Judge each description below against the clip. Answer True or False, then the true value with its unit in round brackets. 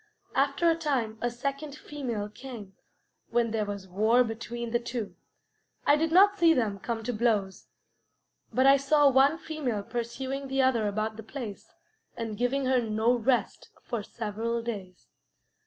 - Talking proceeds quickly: False (155 wpm)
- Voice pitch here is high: True (240 Hz)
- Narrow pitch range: False (3.9 semitones)